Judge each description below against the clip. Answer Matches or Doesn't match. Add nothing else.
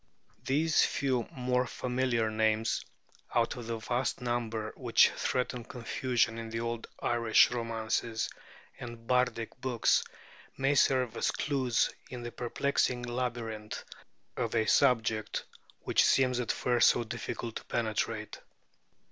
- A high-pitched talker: Doesn't match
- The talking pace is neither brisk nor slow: Doesn't match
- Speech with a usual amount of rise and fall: Doesn't match